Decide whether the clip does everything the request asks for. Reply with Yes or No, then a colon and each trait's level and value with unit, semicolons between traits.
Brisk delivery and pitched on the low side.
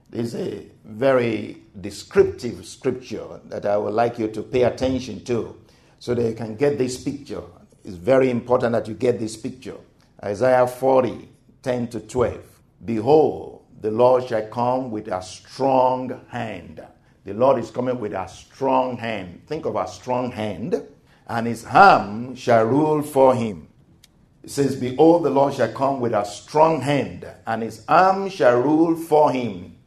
No: average, 165 wpm; low, 125 Hz